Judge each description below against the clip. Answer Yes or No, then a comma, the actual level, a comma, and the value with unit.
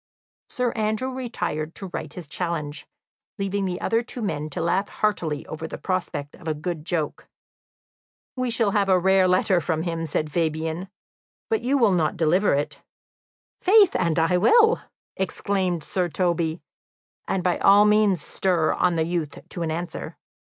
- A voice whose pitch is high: No, medium, 180 Hz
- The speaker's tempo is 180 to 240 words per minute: No, average, 165 wpm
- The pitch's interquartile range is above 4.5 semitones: No, average, 3.9 semitones